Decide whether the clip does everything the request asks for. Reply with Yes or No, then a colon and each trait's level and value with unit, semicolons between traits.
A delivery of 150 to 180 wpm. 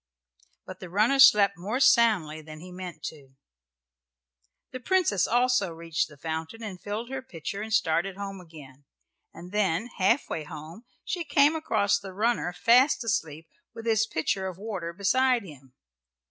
Yes: average, 160 wpm